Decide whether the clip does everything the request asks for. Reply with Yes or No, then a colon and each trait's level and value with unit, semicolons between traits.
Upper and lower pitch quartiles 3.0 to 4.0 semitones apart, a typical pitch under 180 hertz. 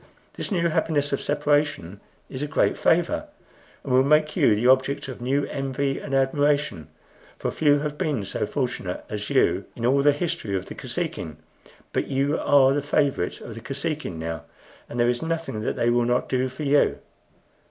Yes: average, 3.5 semitones; medium, 140 Hz